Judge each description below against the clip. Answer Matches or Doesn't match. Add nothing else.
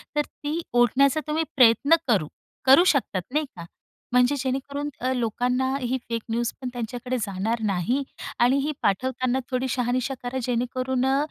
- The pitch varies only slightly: Matches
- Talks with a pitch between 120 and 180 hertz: Doesn't match